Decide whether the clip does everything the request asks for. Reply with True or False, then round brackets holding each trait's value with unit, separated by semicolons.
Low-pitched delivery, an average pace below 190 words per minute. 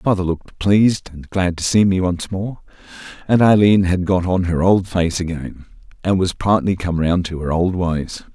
False (90 Hz; 200 wpm)